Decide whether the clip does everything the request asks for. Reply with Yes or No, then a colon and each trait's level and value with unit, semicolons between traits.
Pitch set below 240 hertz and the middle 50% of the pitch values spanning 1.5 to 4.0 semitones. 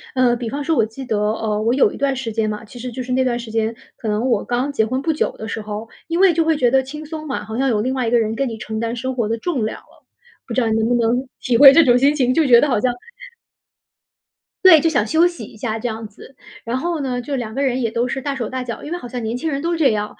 No: high, 245 Hz; average, 3.4 semitones